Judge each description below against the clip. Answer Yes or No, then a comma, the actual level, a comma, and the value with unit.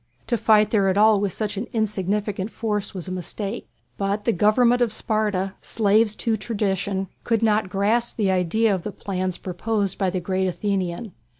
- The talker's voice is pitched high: Yes, high, 205 Hz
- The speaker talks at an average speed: Yes, average, 180 wpm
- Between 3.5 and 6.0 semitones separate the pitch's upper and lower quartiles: No, narrow, 2.4 semitones